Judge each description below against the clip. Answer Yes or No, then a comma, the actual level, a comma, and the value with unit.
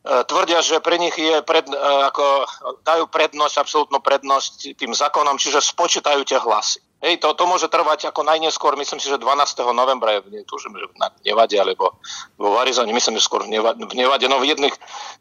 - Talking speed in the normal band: No, fast, 205 wpm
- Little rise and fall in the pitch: No, average, 3.0 semitones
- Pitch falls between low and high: Yes, medium, 155 Hz